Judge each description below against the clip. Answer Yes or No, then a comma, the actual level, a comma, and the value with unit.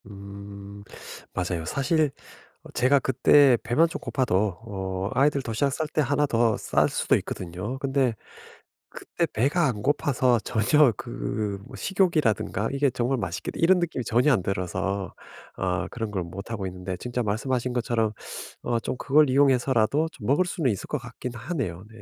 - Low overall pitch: Yes, low, 120 Hz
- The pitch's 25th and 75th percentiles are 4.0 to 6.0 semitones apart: Yes, wide, 5.6 semitones